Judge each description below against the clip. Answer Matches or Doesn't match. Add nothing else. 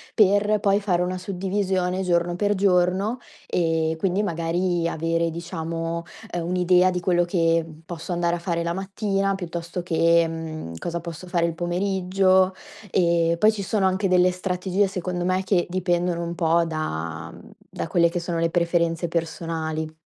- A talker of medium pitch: Matches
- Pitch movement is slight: Matches